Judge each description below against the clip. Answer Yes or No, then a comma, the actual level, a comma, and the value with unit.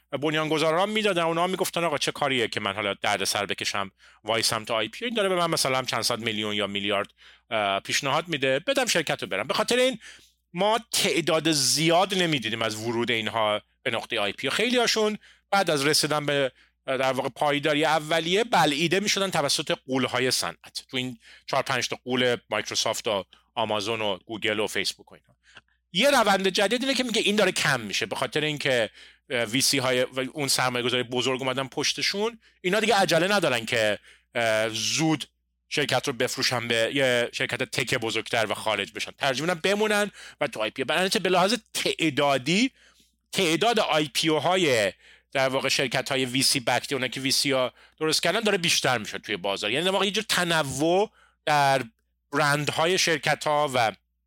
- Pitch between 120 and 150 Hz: Yes, medium, 140 Hz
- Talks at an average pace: No, fast, 180 wpm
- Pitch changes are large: Yes, wide, 6.2 semitones